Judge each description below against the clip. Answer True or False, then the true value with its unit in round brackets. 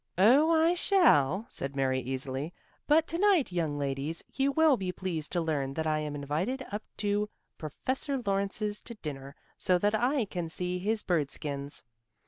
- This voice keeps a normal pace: True (170 wpm)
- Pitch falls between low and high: True (180 Hz)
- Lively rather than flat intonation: True (8.9 semitones)